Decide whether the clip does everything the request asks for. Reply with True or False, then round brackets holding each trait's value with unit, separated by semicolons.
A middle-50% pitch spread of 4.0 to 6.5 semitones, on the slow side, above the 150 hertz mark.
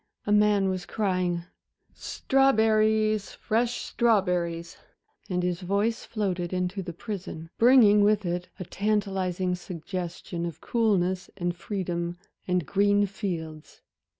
False (3.0 semitones; 120 wpm; 190 Hz)